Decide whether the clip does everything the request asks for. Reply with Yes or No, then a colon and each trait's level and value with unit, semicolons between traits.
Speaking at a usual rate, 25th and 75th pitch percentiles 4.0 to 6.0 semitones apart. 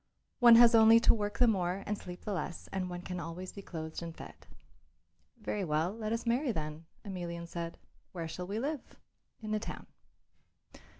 Yes: average, 185 wpm; average, 4.4 semitones